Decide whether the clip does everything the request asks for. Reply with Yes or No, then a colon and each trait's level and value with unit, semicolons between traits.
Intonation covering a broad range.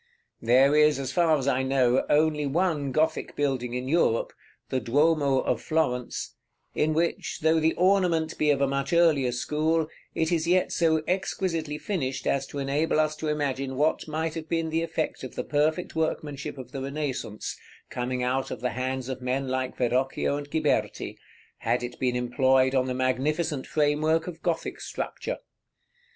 No: average, 3.5 semitones